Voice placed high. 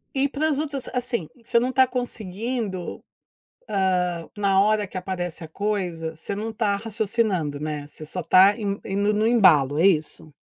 Yes: high, 200 Hz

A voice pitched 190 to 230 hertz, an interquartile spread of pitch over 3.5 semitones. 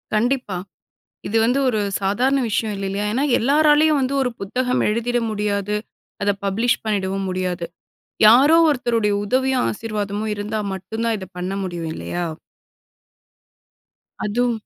Yes: high, 215 Hz; average, 3.9 semitones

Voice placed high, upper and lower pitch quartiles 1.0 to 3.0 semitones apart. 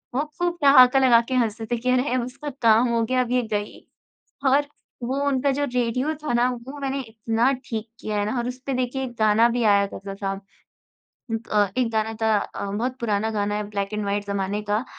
No: high, 235 Hz; average, 3.4 semitones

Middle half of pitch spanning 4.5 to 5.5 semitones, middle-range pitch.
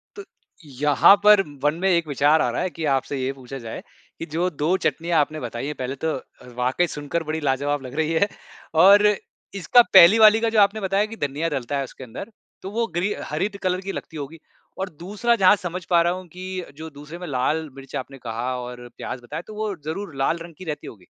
Yes: average, 5.2 semitones; medium, 160 Hz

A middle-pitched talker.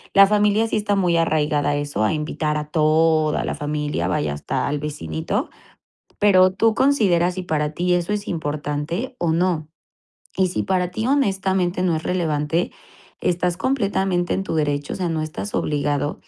Yes: medium, 170 Hz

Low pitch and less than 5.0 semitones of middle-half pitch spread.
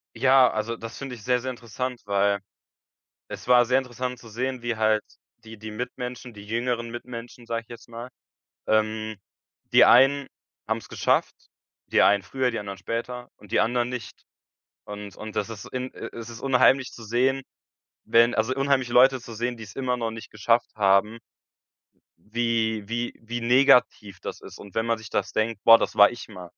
Yes: low, 115 Hz; narrow, 2.4 semitones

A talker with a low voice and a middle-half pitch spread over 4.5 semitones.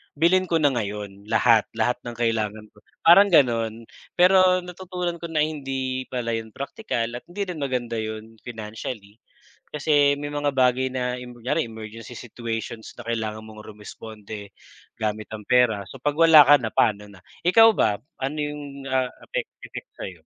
Yes: low, 125 Hz; average, 5.0 semitones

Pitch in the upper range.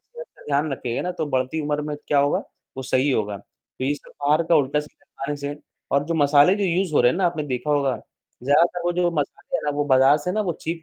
No: medium, 145 Hz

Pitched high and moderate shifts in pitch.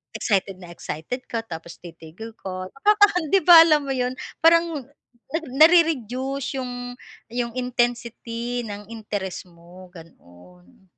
No: high, 235 Hz; wide, 6.7 semitones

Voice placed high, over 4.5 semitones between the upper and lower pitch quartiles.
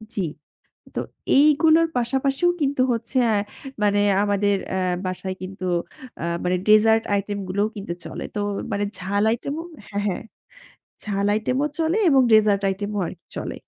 Yes: high, 205 Hz; average, 4.9 semitones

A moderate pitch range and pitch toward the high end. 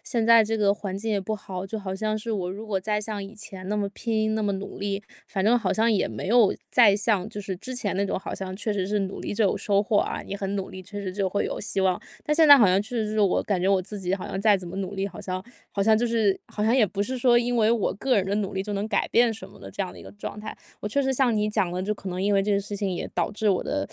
No: narrow, 2.1 semitones; high, 205 Hz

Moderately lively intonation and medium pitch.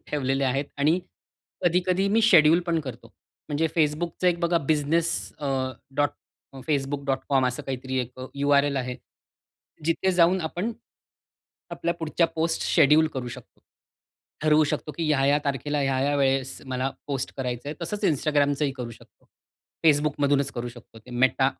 Yes: average, 3.3 semitones; medium, 145 Hz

